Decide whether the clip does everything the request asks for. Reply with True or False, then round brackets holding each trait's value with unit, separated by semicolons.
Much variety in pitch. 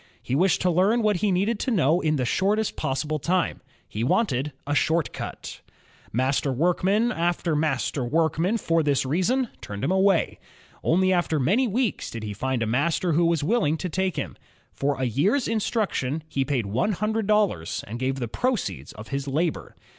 True (6.5 semitones)